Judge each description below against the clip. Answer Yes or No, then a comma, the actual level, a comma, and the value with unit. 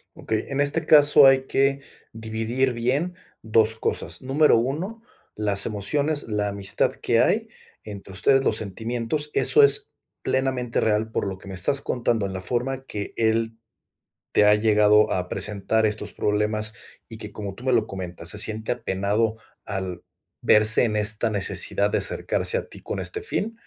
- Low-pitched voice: Yes, low, 110 Hz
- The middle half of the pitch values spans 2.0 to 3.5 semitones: No, average, 4.2 semitones